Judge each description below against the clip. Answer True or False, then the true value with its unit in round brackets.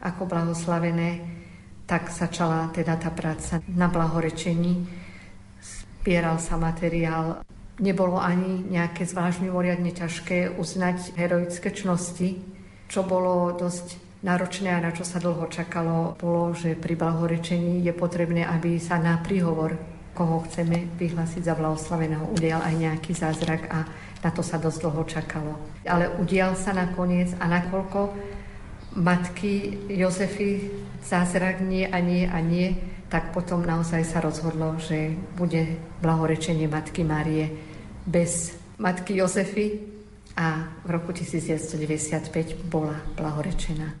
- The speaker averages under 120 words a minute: False (125 wpm)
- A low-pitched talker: False (170 Hz)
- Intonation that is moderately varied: False (1.7 semitones)